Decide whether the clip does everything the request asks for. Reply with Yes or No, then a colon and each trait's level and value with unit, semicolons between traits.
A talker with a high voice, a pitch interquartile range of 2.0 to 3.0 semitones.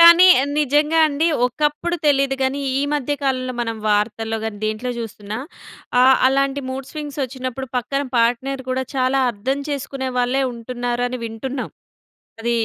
Yes: very high, 260 Hz; narrow, 2.5 semitones